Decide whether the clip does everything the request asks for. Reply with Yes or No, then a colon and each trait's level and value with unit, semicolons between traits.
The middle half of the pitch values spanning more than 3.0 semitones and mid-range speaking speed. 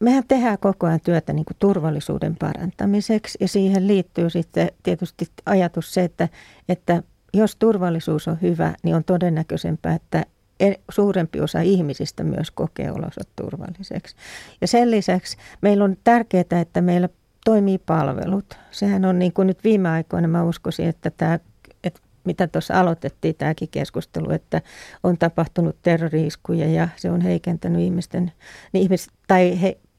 No: narrow, 2.6 semitones; average, 145 wpm